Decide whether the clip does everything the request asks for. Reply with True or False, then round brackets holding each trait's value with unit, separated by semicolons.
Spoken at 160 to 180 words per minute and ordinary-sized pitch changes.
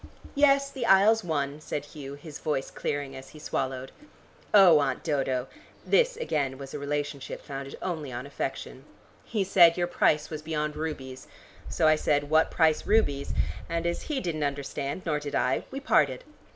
True (170 wpm; 3.8 semitones)